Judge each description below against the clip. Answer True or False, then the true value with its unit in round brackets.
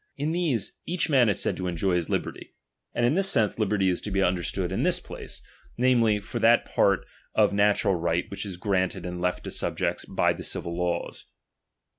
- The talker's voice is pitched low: True (100 Hz)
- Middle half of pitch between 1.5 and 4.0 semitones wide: False (4.5 semitones)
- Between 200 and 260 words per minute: True (205 wpm)